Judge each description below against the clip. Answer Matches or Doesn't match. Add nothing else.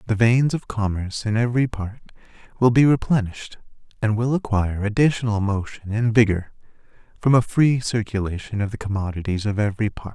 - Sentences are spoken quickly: Doesn't match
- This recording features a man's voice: Matches